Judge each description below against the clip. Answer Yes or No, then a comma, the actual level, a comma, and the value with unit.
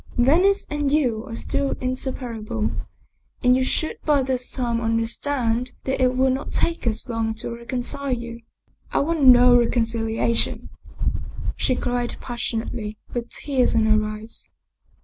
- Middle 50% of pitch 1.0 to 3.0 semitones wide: Yes, narrow, 2.5 semitones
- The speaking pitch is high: Yes, high, 245 Hz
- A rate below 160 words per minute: Yes, average, 145 wpm